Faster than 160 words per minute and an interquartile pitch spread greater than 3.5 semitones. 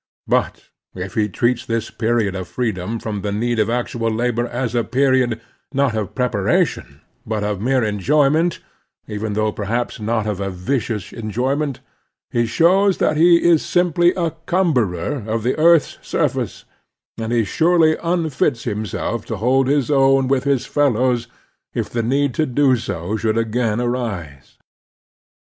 No: average, 155 wpm; average, 4.3 semitones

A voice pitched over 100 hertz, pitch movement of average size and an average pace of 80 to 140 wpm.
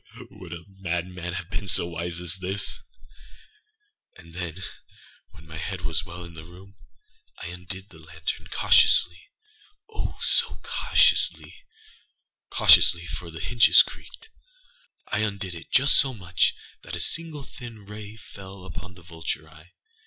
No: very low, 90 Hz; average, 3.8 semitones; slow, 135 wpm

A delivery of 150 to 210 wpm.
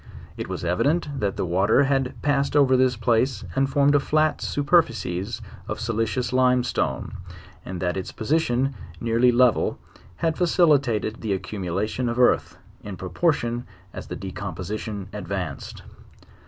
No: average, 140 wpm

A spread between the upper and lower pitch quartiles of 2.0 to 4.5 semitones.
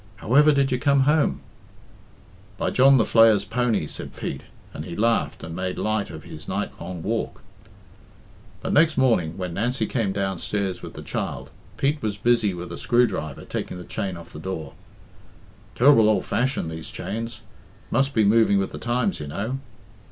No: average, 5.1 semitones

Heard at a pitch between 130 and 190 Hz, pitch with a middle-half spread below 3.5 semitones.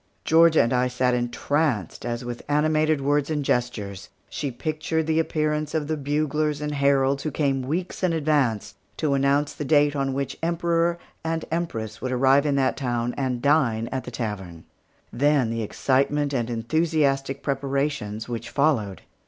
No: medium, 140 Hz; average, 3.8 semitones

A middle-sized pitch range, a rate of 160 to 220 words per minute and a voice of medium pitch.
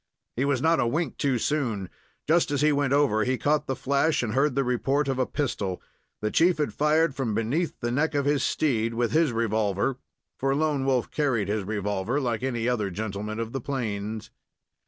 No: average, 4.6 semitones; average, 200 wpm; low, 130 Hz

